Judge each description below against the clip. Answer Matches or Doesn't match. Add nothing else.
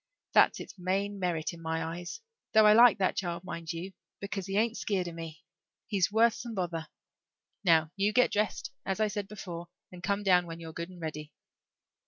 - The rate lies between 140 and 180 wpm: Doesn't match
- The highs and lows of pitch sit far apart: Doesn't match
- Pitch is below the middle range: Doesn't match